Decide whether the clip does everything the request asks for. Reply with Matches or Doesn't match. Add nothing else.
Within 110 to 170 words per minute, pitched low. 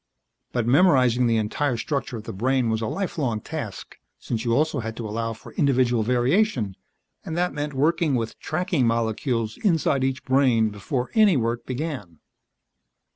Matches